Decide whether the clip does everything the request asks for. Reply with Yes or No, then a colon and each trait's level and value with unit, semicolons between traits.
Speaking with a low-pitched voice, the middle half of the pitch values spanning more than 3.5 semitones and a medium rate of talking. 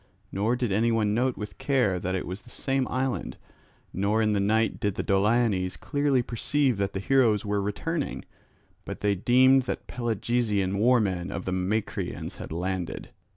Yes: low, 110 Hz; average, 4.1 semitones; average, 170 wpm